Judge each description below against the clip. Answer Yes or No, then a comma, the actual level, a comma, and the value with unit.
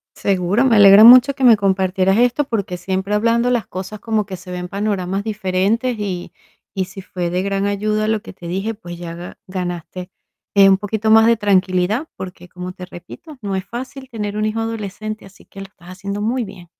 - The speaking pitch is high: Yes, high, 200 Hz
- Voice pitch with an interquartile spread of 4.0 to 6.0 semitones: No, average, 3.0 semitones